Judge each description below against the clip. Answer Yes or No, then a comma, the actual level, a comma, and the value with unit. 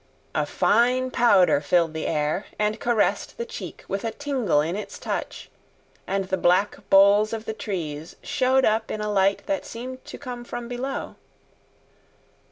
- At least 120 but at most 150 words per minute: No, average, 165 wpm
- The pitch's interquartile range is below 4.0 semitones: No, average, 4.5 semitones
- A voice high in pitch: Yes, high, 215 Hz